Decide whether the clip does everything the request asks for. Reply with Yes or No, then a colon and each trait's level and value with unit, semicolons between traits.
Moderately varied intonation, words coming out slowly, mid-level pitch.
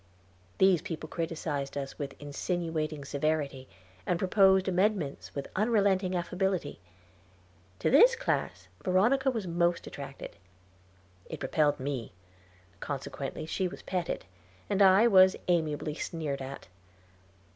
Yes: average, 4.8 semitones; slow, 115 wpm; medium, 170 Hz